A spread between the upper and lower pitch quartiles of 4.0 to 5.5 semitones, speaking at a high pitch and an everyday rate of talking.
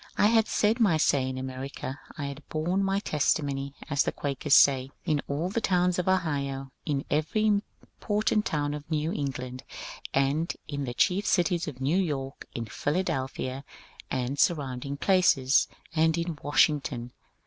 No: average, 4.5 semitones; medium, 145 Hz; average, 160 wpm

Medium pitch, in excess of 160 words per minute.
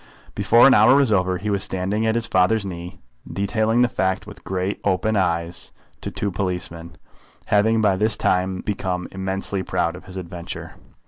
No: very low, 95 Hz; average, 175 wpm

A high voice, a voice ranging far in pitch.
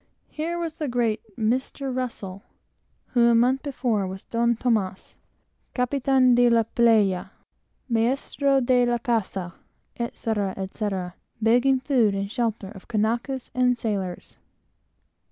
No: high, 235 Hz; average, 3.3 semitones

